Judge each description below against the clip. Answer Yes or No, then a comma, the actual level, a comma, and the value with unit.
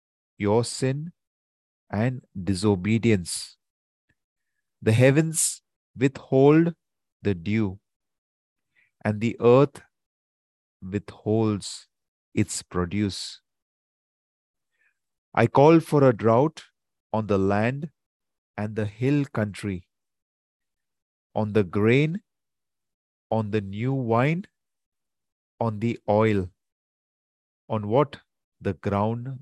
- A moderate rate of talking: No, slow, 85 wpm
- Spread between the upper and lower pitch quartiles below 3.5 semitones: No, average, 4.3 semitones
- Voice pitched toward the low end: Yes, low, 105 Hz